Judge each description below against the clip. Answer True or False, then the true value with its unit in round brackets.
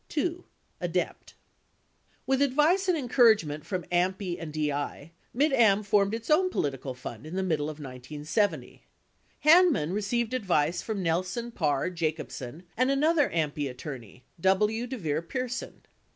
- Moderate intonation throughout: False (8.4 semitones)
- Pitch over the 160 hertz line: True (185 Hz)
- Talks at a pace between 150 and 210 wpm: False (140 wpm)